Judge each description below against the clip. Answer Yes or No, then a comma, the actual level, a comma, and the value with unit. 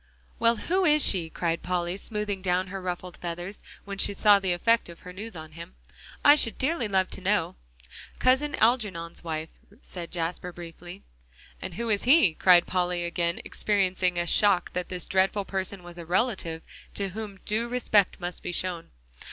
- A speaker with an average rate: Yes, average, 175 wpm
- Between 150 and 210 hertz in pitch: Yes, medium, 185 Hz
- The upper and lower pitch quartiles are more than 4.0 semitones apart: No, average, 3.2 semitones